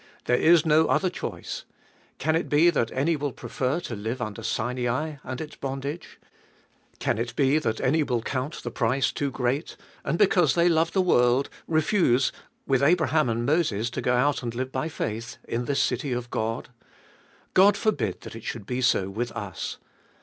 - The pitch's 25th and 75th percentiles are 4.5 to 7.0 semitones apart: Yes, average, 4.8 semitones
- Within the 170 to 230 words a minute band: Yes, average, 185 wpm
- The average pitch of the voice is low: Yes, low, 130 Hz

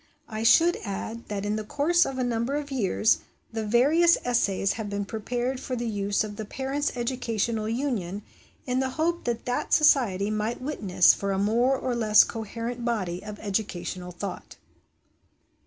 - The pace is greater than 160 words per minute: Yes, average, 170 wpm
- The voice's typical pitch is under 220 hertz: No, high, 230 Hz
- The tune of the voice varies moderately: Yes, average, 3.8 semitones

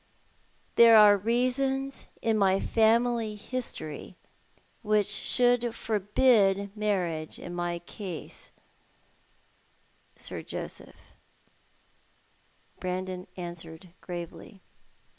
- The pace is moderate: No, slow, 75 wpm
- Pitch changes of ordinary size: Yes, average, 4.3 semitones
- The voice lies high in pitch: Yes, high, 205 Hz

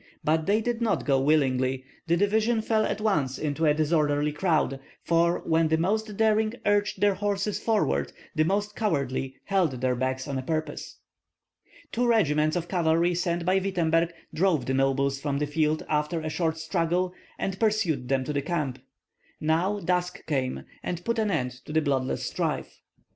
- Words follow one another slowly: No, average, 170 wpm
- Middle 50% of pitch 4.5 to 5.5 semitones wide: Yes, average, 5.2 semitones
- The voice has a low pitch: No, medium, 165 Hz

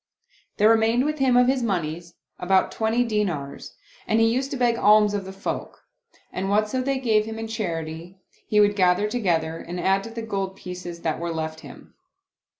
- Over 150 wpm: Yes, average, 190 wpm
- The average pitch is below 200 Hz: No, high, 205 Hz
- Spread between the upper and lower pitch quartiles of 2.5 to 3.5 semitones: No, average, 4.3 semitones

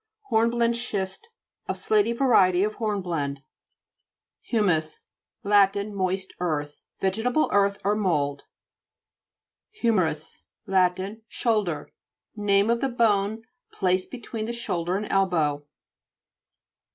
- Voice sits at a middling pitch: No, high, 200 Hz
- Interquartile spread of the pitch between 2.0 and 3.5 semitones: No, average, 4.1 semitones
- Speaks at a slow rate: Yes, slow, 105 wpm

